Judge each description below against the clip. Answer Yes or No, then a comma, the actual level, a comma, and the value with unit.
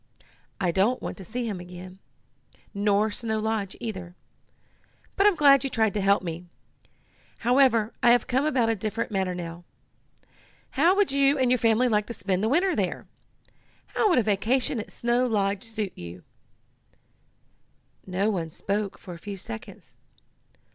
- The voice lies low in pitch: No, high, 215 Hz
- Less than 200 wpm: Yes, average, 160 wpm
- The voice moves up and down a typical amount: Yes, average, 4.5 semitones